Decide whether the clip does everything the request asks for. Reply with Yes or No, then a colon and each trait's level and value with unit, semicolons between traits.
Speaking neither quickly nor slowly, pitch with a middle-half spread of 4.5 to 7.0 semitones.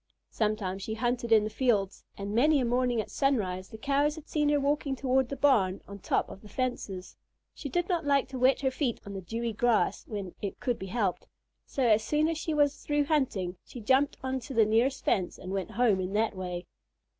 No: fast, 225 wpm; wide, 5.4 semitones